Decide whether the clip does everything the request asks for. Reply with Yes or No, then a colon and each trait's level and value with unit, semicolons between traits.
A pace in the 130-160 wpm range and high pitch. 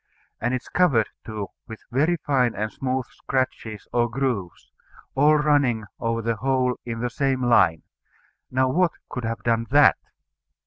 No: average, 155 wpm; low, 125 Hz